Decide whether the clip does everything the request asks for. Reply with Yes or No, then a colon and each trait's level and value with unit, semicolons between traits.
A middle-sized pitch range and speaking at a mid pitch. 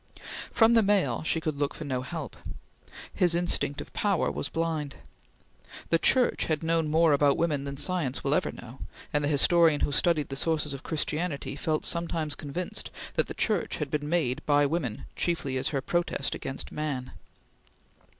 Yes: average, 3.1 semitones; medium, 155 Hz